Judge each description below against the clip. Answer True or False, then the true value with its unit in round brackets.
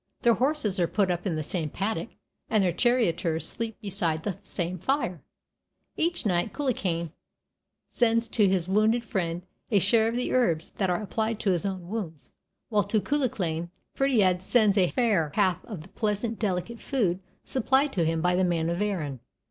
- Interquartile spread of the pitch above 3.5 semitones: True (4.7 semitones)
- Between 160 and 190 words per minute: True (180 wpm)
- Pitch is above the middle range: True (195 Hz)